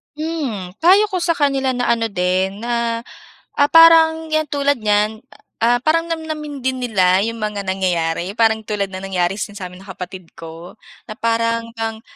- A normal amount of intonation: No, wide, 6.8 semitones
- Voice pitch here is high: Yes, high, 230 Hz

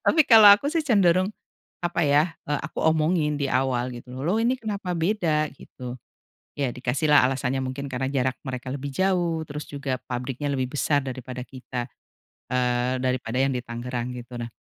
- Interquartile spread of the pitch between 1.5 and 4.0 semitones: No, average, 4.8 semitones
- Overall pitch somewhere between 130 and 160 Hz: Yes, low, 135 Hz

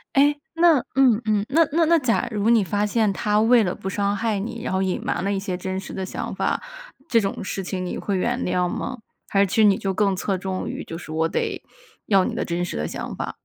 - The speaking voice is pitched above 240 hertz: No, high, 200 Hz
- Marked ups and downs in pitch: No, average, 3.3 semitones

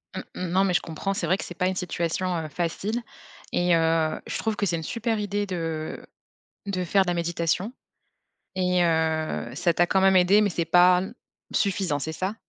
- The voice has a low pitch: No, medium, 180 Hz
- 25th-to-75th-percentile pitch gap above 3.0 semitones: No, average, 2.7 semitones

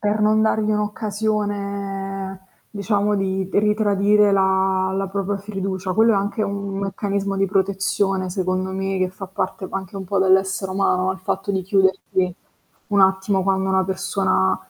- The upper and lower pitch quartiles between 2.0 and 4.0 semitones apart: No, narrow, 1.2 semitones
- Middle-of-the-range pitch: No, high, 195 Hz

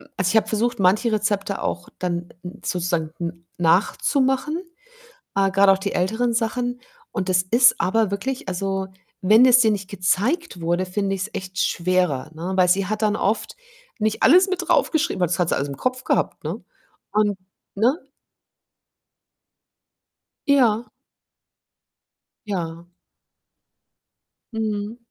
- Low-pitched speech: No, high, 200 Hz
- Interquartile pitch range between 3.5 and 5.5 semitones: Yes, average, 4.0 semitones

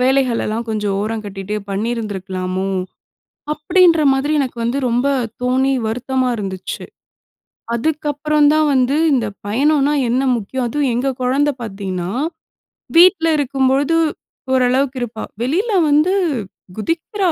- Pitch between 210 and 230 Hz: No, very high, 255 Hz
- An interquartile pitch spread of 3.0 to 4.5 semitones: No, average, 5.0 semitones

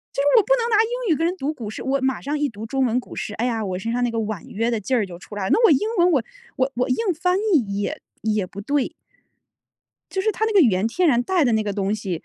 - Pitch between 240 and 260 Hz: Yes, very high, 250 Hz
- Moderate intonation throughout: No, wide, 7.3 semitones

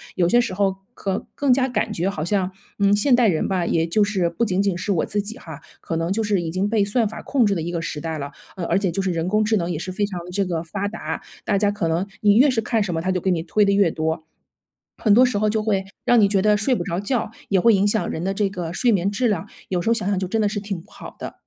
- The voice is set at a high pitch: Yes, high, 200 Hz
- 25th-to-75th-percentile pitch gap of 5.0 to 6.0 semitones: No, average, 3.4 semitones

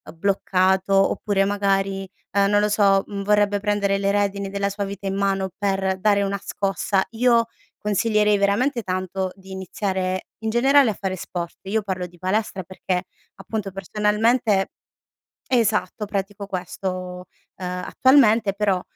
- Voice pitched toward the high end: Yes, high, 200 Hz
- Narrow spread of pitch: Yes, narrow, 1.6 semitones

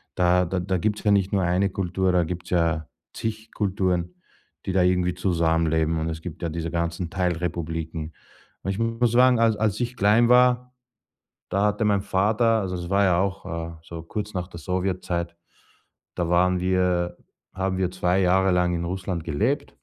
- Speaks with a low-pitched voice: Yes, very low, 90 Hz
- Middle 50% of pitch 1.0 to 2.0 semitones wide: No, narrow, 2.6 semitones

